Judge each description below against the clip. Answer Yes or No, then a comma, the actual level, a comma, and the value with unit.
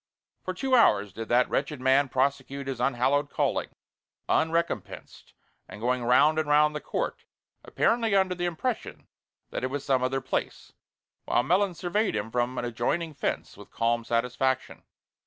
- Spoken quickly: No, average, 155 wpm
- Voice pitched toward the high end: No, low, 135 Hz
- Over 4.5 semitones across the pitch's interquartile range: Yes, average, 5.2 semitones